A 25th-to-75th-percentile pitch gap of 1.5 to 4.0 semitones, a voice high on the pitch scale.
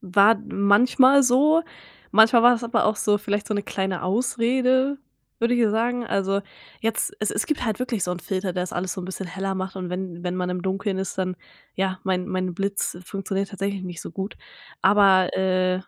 Yes: average, 3.6 semitones; high, 195 Hz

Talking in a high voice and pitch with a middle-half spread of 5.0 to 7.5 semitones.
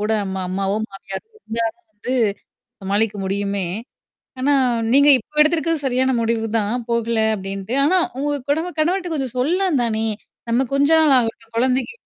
Yes: high, 240 Hz; wide, 5.4 semitones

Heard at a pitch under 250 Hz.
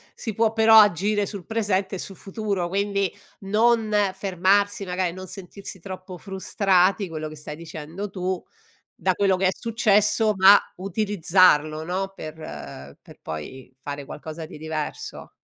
Yes: high, 190 Hz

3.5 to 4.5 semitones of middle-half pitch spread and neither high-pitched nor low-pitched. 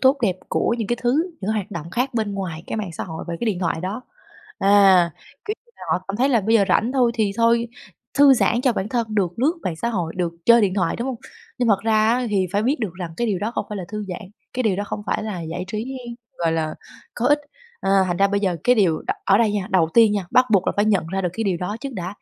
No: average, 4.2 semitones; high, 205 Hz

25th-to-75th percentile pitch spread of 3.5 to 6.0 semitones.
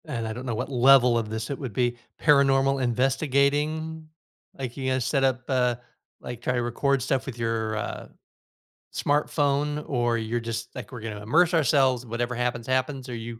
No: average, 2.8 semitones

